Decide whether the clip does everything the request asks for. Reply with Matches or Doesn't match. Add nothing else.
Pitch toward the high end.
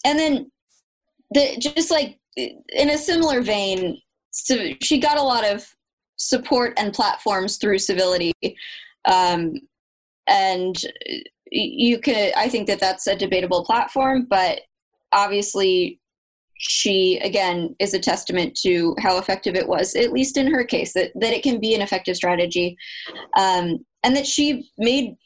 Matches